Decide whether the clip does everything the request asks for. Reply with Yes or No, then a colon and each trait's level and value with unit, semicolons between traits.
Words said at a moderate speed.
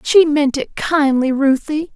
Yes: average, 155 wpm